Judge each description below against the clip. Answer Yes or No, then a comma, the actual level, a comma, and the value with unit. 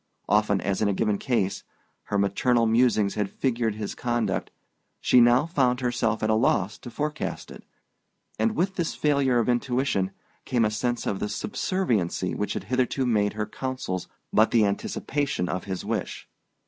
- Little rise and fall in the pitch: No, average, 3.9 semitones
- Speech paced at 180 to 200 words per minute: No, average, 170 wpm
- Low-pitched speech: Yes, low, 115 Hz